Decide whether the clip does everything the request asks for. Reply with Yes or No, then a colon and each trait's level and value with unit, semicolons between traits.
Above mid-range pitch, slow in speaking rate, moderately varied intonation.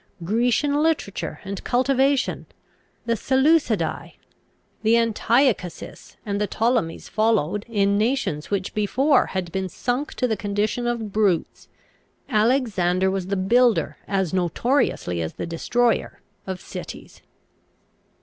Yes: high, 215 Hz; slow, 115 wpm; average, 4.5 semitones